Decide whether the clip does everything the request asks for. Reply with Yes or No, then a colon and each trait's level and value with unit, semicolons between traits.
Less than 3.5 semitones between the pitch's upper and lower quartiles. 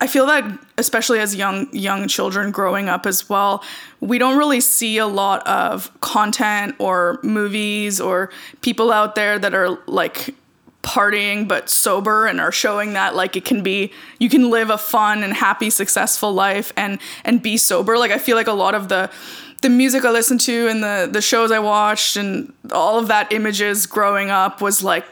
Yes: average, 3.0 semitones